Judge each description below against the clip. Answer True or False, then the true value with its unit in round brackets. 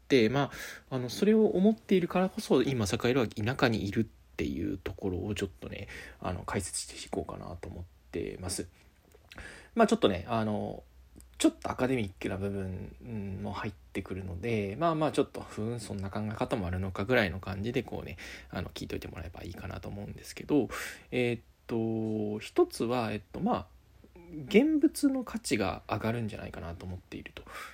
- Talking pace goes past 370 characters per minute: True (385 characters per minute)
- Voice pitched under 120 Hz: True (105 Hz)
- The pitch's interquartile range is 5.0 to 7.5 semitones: True (5.3 semitones)